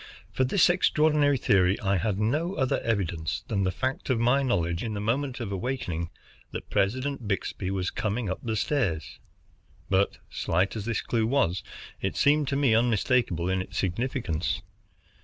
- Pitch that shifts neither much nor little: No, wide, 5.7 semitones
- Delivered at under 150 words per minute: No, average, 165 wpm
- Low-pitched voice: Yes, low, 110 Hz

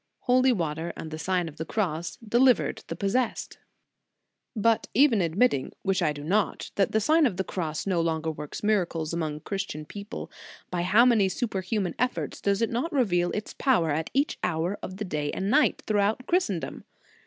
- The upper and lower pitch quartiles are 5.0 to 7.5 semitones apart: Yes, wide, 5.6 semitones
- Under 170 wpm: No, average, 185 wpm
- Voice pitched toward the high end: Yes, high, 195 Hz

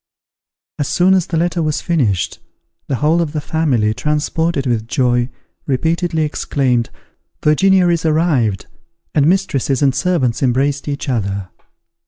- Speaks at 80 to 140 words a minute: Yes, slow, 135 wpm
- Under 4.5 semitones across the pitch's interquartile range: No, average, 4.8 semitones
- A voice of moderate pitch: Yes, medium, 145 Hz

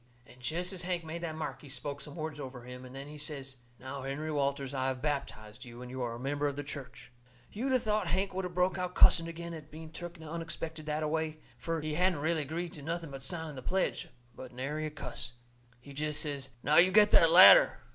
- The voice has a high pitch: No, medium, 155 Hz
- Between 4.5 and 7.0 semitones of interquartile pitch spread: No, average, 3.7 semitones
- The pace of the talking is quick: Yes, fast, 240 wpm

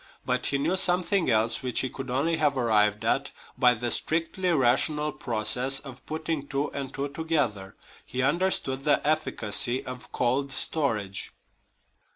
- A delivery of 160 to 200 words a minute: No, average, 150 wpm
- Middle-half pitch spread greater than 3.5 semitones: Yes, average, 4.1 semitones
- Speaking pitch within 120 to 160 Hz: Yes, low, 135 Hz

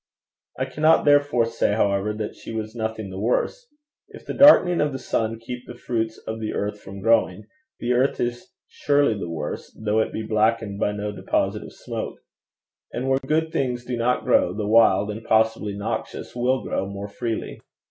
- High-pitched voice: No, low, 110 Hz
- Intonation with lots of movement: No, average, 3.0 semitones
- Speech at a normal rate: Yes, average, 190 wpm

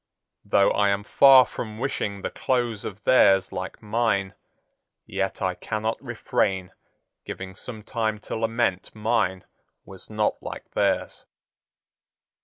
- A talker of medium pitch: No, low, 105 Hz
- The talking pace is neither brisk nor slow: No, slow, 125 wpm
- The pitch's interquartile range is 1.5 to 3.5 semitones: Yes, average, 2.9 semitones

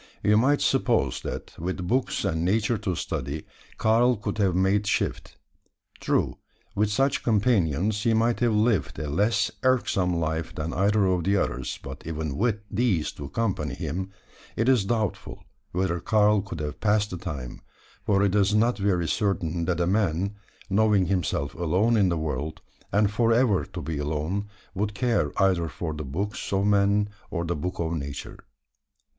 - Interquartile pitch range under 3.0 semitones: No, average, 4.5 semitones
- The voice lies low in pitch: Yes, very low, 95 Hz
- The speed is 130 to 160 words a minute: No, average, 170 wpm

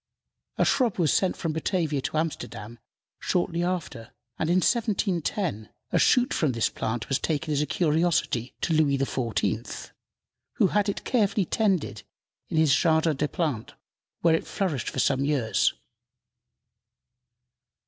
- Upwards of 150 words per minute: No, average, 140 wpm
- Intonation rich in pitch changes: No, average, 4.8 semitones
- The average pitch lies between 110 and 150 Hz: No, medium, 160 Hz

